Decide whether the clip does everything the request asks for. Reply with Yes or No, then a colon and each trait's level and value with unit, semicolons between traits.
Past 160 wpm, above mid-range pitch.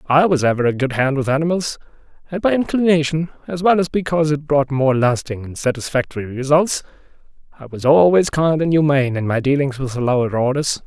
No: average, 195 wpm; medium, 145 Hz